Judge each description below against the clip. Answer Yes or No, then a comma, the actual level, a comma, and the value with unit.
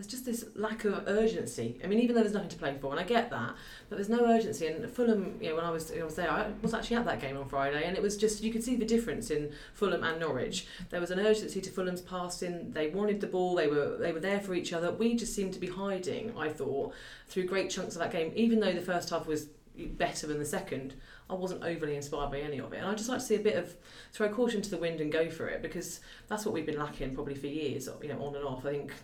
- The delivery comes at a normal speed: No, fast, 285 wpm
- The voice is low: No, medium, 180 Hz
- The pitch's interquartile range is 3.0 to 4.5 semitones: No, average, 5.3 semitones